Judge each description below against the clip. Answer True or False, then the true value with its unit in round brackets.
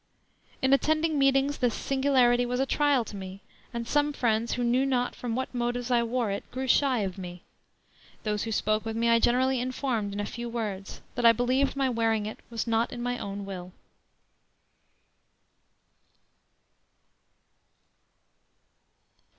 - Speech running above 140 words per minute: True (155 wpm)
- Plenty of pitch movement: False (3.1 semitones)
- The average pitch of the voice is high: True (240 Hz)